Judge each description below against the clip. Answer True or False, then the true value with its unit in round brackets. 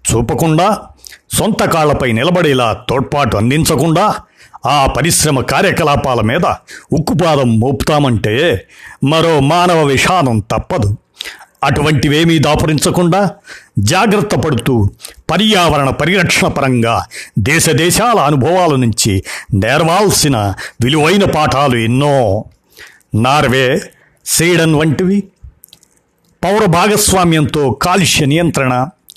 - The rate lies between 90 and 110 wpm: False (75 wpm)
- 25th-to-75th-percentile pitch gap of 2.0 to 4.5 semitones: False (5.2 semitones)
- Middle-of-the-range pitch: True (150 Hz)